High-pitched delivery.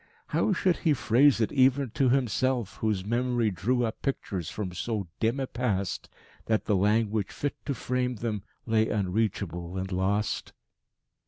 No: low, 110 Hz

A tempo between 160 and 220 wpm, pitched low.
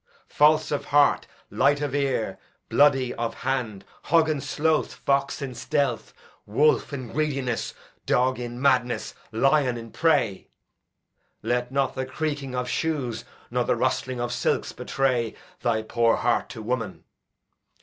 No: average, 140 wpm; low, 130 Hz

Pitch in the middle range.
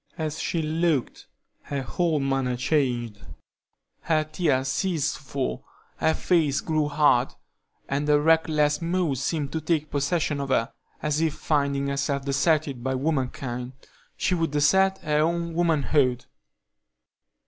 Yes: medium, 150 Hz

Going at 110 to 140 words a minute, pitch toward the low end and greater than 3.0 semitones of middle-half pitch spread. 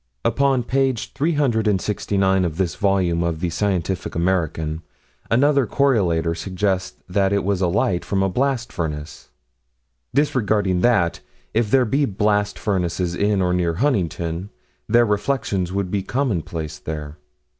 Yes: slow, 135 wpm; very low, 95 Hz; average, 4.8 semitones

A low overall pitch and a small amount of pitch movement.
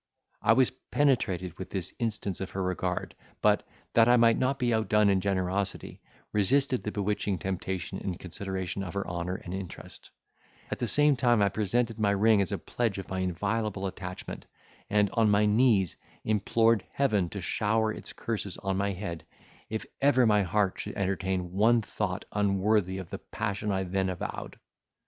No: low, 100 Hz; average, 3.0 semitones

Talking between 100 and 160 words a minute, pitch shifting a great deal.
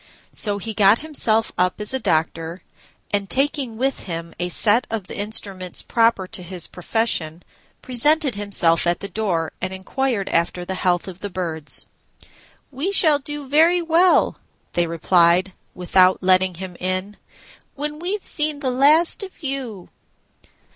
Yes: average, 150 wpm; wide, 6.9 semitones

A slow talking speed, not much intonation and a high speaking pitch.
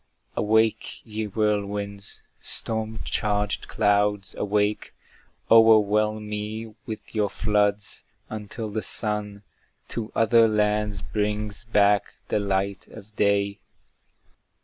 No: slow, 100 wpm; narrow, 1.1 semitones; low, 105 Hz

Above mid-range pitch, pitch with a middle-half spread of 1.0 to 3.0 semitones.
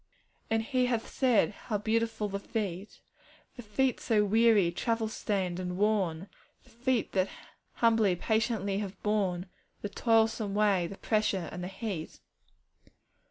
Yes: high, 210 Hz; average, 2.7 semitones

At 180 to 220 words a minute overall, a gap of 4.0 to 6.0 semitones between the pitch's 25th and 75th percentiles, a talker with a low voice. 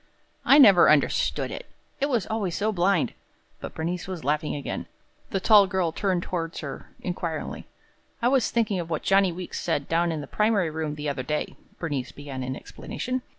No: average, 185 wpm; average, 4.8 semitones; medium, 175 Hz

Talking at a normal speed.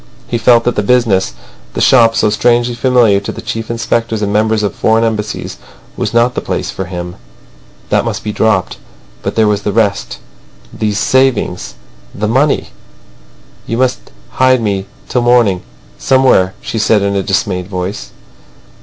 Yes: average, 165 wpm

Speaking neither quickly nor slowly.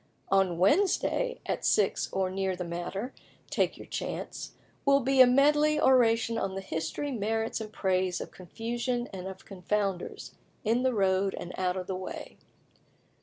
Yes: average, 160 wpm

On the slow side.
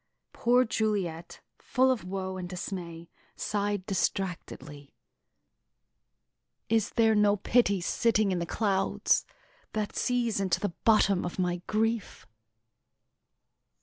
Yes: slow, 110 wpm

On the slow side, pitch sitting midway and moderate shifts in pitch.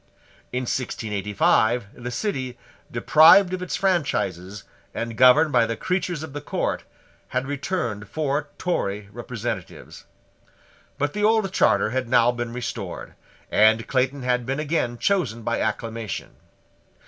No: slow, 130 wpm; low, 125 Hz; average, 4.9 semitones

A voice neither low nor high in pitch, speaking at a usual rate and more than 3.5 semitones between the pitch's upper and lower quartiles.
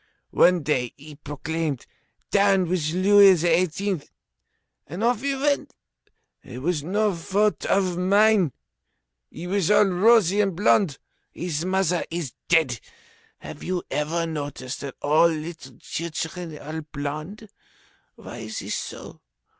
No: medium, 170 Hz; slow, 130 wpm; average, 4.4 semitones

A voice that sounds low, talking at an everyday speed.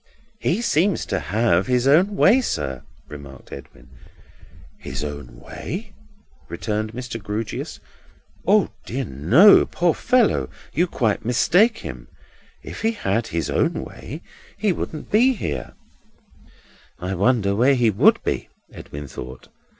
No: low, 115 Hz; slow, 130 wpm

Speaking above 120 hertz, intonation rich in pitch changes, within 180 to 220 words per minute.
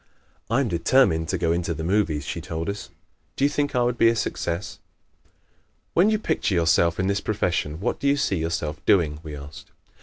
No: very low, 90 Hz; wide, 6.1 semitones; fast, 205 wpm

